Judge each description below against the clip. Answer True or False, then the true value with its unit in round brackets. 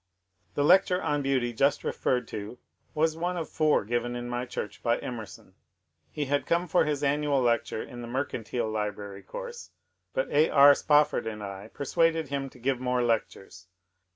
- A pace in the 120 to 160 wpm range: False (175 wpm)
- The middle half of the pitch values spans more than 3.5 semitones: True (4.2 semitones)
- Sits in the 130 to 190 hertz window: True (135 Hz)